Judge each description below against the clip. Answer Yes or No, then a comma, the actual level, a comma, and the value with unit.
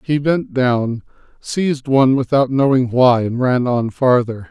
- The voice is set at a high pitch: No, low, 130 Hz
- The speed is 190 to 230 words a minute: No, average, 160 wpm